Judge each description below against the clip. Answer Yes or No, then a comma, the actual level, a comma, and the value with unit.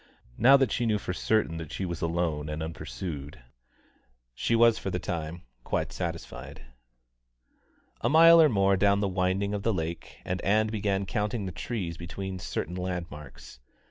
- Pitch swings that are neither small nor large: Yes, average, 4.0 semitones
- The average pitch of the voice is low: Yes, very low, 95 Hz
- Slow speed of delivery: No, average, 160 wpm